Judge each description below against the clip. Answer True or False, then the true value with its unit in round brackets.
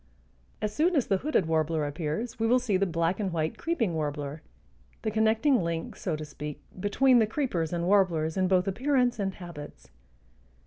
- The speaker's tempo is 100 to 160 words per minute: False (180 wpm)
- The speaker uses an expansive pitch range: True (5.8 semitones)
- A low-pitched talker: False (185 Hz)